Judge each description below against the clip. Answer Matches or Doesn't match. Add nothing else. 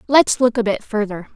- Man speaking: Doesn't match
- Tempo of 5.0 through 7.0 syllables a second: Matches